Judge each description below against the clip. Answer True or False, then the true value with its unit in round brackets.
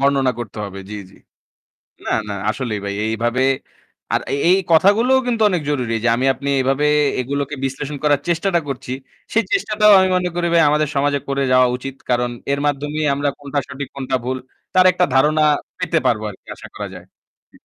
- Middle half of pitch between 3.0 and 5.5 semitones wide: True (3.5 semitones)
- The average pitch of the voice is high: False (140 Hz)